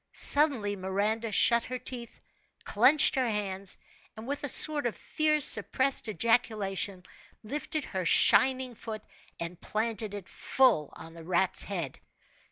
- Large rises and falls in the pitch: No, average, 5.0 semitones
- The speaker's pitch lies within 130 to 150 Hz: No, high, 220 Hz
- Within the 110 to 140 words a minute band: Yes, slow, 135 wpm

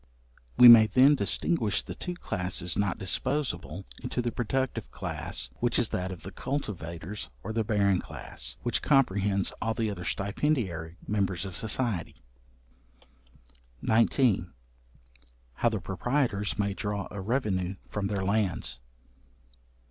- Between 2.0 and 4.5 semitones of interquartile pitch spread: Yes, average, 4.1 semitones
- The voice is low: Yes, low, 105 Hz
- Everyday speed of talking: No, slow, 130 wpm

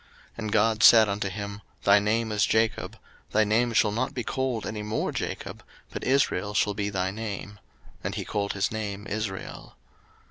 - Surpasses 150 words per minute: Yes, average, 180 wpm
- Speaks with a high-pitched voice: No, low, 105 Hz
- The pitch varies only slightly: Yes, narrow, 1.8 semitones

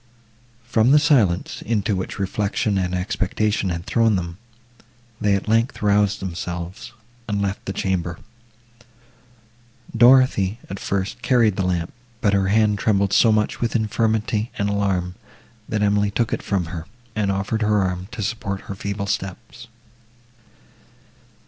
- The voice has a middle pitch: No, low, 100 Hz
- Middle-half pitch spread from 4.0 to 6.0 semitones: No, narrow, 2.5 semitones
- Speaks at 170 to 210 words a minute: No, average, 140 wpm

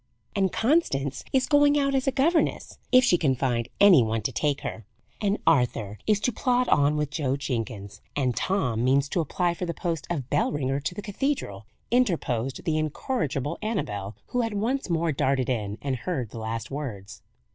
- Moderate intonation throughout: No, wide, 8.7 semitones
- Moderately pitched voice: Yes, medium, 145 Hz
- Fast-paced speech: No, average, 190 wpm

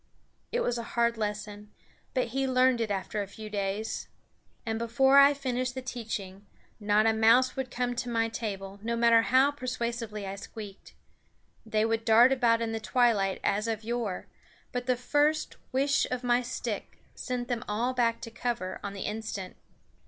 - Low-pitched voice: No, high, 230 Hz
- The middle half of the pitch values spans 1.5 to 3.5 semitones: Yes, average, 2.9 semitones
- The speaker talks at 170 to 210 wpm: Yes, average, 175 wpm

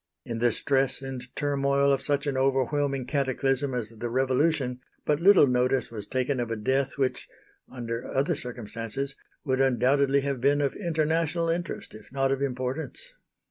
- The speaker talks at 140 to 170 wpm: Yes, average, 160 wpm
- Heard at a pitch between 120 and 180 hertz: Yes, low, 135 Hz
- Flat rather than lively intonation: Yes, narrow, 2.2 semitones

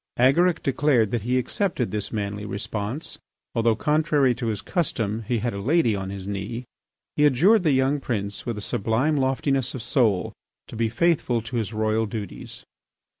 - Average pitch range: Yes, average, 4.3 semitones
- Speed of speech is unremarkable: Yes, average, 175 wpm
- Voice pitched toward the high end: No, low, 120 Hz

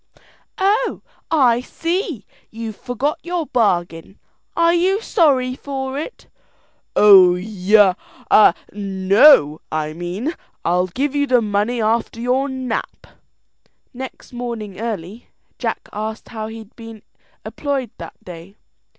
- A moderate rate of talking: No, slow, 115 wpm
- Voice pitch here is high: Yes, high, 230 Hz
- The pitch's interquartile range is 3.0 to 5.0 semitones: No, wide, 5.4 semitones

